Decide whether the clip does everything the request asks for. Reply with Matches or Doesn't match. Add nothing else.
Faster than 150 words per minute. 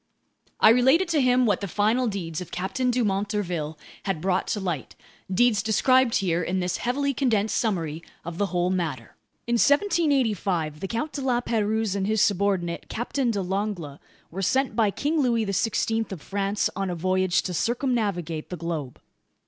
Matches